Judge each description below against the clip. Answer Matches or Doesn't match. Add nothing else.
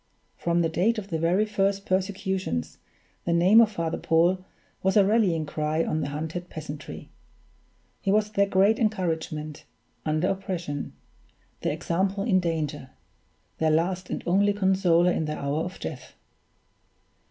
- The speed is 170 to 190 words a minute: Doesn't match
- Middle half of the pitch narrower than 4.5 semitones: Matches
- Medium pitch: Matches